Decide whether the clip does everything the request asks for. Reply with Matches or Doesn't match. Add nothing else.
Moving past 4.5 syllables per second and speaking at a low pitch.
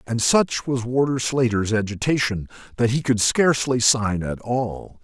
Doesn't match